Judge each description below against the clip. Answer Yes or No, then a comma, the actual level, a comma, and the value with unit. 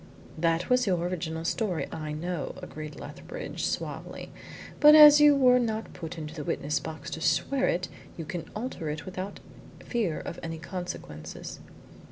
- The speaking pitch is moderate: Yes, medium, 175 Hz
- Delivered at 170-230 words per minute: No, average, 160 wpm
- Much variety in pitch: Yes, wide, 6.3 semitones